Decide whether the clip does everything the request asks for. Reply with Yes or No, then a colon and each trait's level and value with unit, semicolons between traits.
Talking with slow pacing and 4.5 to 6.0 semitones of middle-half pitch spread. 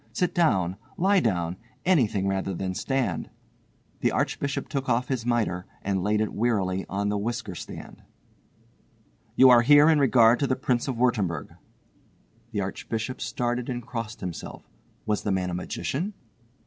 No: average, 155 wpm; average, 5.1 semitones